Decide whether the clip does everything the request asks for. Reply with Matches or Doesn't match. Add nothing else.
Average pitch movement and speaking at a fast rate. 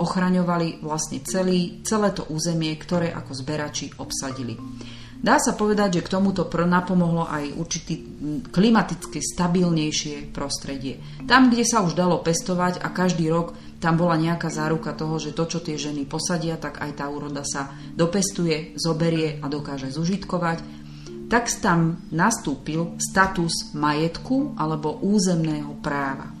Doesn't match